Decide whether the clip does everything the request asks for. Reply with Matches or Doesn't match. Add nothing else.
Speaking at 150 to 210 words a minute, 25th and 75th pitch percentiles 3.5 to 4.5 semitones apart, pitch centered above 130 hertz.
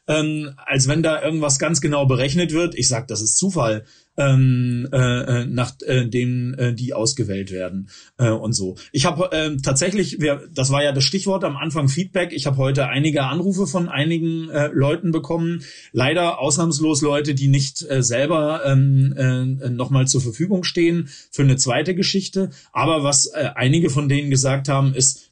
Matches